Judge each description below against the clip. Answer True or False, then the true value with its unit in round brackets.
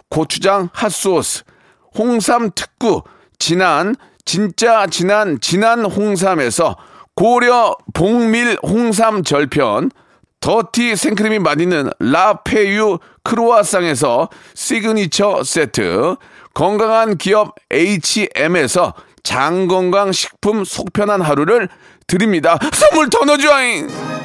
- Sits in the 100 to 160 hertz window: False (205 Hz)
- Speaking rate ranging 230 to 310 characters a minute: False (210 characters per minute)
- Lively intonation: False (3.8 semitones)